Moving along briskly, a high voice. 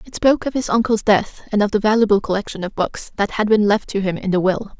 Yes: fast, 275 wpm; high, 210 Hz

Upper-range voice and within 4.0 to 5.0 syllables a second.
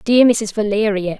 Yes: high, 210 Hz; 4.6 syllables/s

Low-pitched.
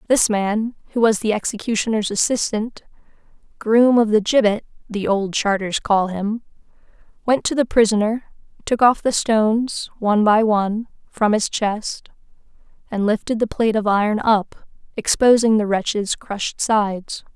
No: high, 215 Hz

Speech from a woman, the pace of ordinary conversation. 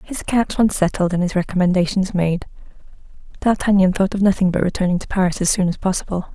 Yes: female; average, 190 wpm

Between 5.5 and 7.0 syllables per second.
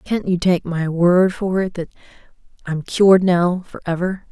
No: 4.4 syllables/s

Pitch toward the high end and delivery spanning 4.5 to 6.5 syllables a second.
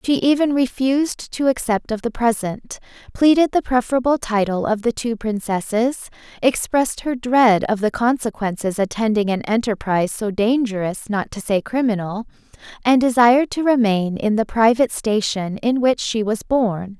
Yes: high, 230 Hz; 4.9 syllables/s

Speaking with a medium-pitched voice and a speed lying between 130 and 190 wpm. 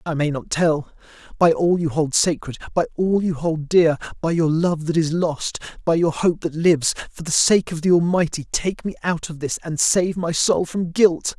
No: medium, 165 Hz; average, 200 wpm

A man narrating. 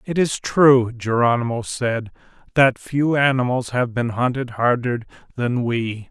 Yes: male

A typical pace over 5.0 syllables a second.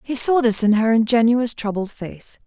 No: 4.7 syllables/s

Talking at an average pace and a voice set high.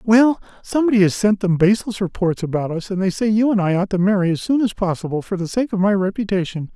No: fast, 240 wpm; high, 195 Hz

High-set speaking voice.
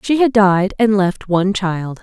Yes: high, 200 Hz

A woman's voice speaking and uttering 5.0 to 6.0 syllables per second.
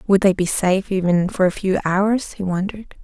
Yes: female; 5.3 syllables/s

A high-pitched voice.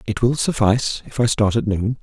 No: low, 110 Hz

